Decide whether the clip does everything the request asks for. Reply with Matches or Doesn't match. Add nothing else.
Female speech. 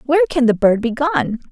Matches